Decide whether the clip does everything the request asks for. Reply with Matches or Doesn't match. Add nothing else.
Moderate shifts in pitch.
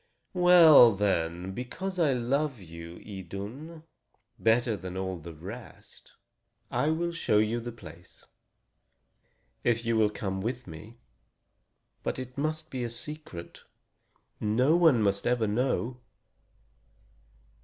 Doesn't match